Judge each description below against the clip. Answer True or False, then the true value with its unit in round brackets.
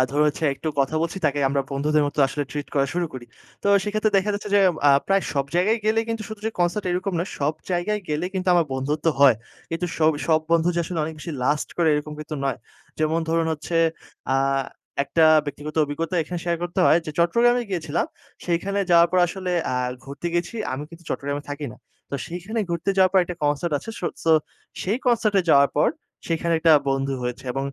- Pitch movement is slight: False (3.9 semitones)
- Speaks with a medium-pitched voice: True (165 Hz)